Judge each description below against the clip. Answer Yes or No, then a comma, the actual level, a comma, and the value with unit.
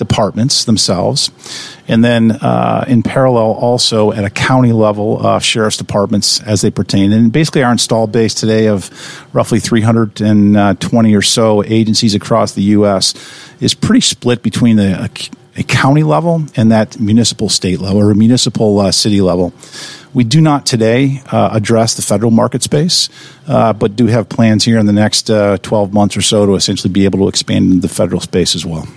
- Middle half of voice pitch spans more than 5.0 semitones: No, average, 2.9 semitones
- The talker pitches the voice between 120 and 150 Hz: No, low, 110 Hz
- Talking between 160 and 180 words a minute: No, average, 190 wpm